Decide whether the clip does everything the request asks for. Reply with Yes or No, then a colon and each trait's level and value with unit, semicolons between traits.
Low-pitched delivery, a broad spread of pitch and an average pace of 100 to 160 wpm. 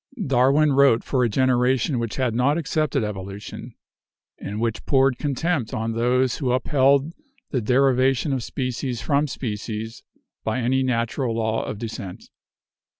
No: low, 125 Hz; average, 3.0 semitones; average, 140 wpm